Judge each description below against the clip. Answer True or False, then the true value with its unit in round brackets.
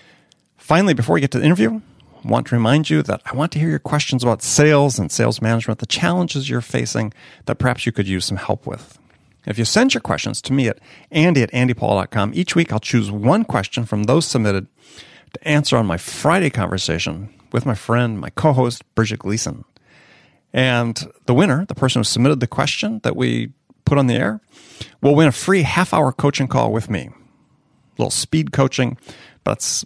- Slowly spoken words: False (200 wpm)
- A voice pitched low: True (125 Hz)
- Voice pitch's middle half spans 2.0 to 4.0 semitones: False (4.9 semitones)